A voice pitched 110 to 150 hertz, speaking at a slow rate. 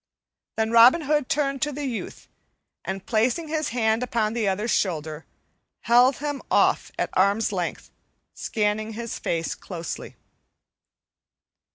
No: high, 225 Hz; slow, 130 wpm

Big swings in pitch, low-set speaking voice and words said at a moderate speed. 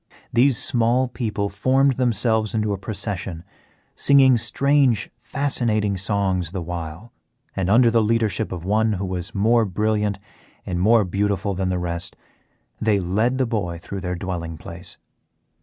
No: average, 4.0 semitones; low, 105 Hz; average, 145 wpm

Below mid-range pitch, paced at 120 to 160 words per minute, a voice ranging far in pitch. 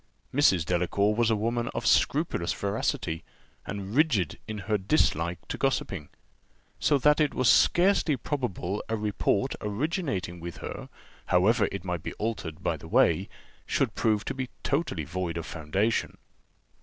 Yes: low, 105 Hz; average, 150 wpm; wide, 6.2 semitones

